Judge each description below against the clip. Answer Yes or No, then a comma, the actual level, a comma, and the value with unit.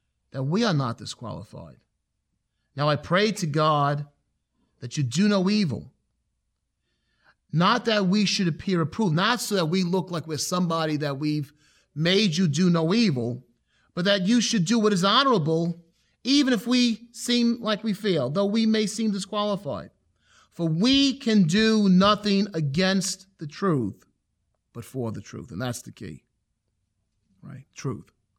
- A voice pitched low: No, medium, 185 Hz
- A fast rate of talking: No, average, 155 wpm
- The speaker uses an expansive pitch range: Yes, wide, 6.0 semitones